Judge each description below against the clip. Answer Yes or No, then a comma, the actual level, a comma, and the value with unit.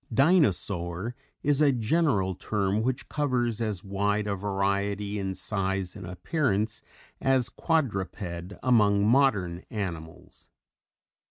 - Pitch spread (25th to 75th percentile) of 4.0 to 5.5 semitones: Yes, average, 4.4 semitones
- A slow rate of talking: Yes, slow, 105 wpm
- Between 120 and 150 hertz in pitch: No, low, 105 Hz